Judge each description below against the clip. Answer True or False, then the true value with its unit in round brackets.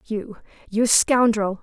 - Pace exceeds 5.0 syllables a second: False (3.2 syllables/s)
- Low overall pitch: False (220 Hz)